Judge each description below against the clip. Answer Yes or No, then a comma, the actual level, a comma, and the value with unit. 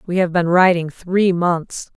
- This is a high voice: No, medium, 175 Hz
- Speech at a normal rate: Yes, average, 180 wpm